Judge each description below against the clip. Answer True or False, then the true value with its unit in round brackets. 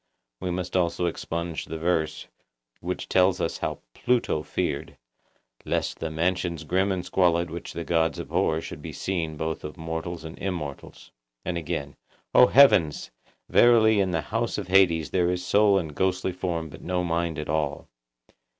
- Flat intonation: True (2.3 semitones)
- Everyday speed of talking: True (165 wpm)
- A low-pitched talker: True (85 Hz)